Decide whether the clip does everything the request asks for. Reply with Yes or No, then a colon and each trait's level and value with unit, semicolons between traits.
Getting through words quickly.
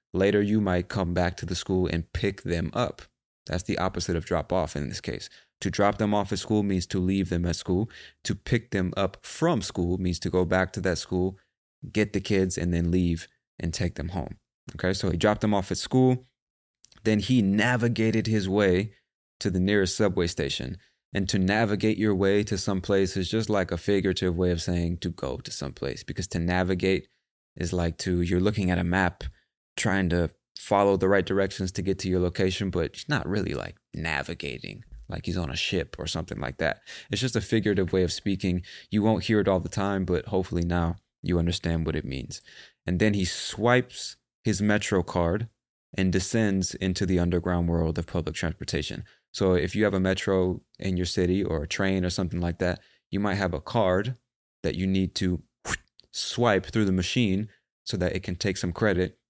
Yes: fast, 210 wpm